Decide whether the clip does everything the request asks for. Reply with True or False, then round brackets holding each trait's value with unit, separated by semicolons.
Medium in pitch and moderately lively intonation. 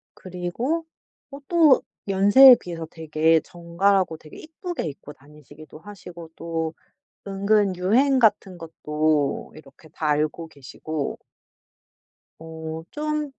True (170 Hz; 4.7 semitones)